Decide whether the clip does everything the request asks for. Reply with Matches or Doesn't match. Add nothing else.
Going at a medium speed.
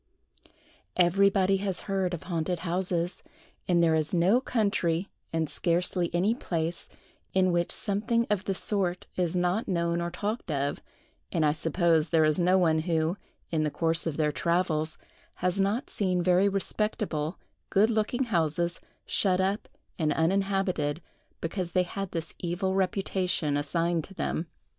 Matches